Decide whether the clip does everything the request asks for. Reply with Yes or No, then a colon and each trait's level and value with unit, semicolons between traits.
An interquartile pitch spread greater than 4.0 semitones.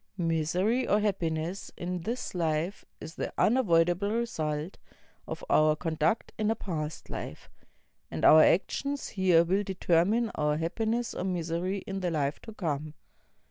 Yes: average, 4.4 semitones